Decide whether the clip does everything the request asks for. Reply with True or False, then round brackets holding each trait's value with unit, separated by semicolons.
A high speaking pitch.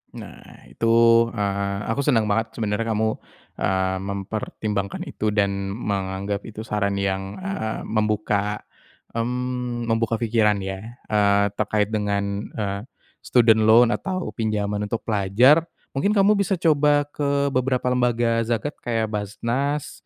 False (110 Hz)